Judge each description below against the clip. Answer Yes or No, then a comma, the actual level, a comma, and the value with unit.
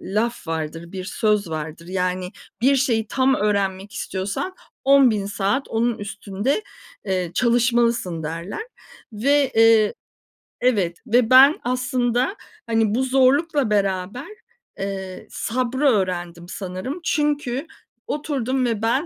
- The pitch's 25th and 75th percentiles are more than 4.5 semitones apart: Yes, average, 5.3 semitones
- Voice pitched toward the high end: Yes, high, 225 Hz